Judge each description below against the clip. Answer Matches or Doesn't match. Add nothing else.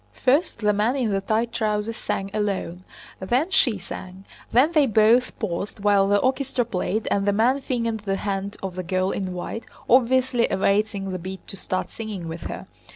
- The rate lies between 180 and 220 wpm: Matches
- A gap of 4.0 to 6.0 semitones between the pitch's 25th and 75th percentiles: Doesn't match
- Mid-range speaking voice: Doesn't match